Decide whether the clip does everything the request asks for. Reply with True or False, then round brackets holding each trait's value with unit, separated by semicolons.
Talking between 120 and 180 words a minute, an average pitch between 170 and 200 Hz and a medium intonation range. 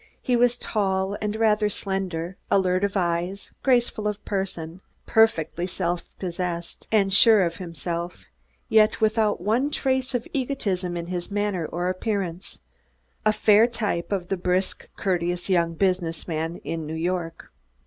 True (140 wpm; 190 Hz; 3.6 semitones)